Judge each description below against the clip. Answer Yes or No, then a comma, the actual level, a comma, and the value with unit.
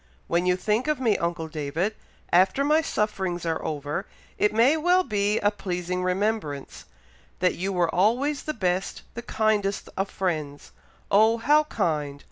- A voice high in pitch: Yes, high, 195 Hz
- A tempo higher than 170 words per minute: No, average, 155 wpm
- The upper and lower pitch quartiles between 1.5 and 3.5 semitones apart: No, average, 4.4 semitones